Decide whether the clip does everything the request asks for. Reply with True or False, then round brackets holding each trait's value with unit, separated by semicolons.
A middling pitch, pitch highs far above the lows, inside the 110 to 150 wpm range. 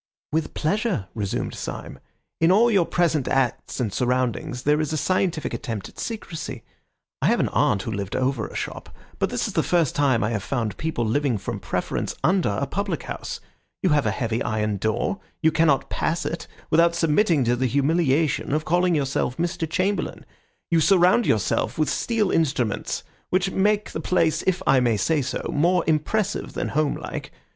False (150 Hz; 6.0 semitones; 180 wpm)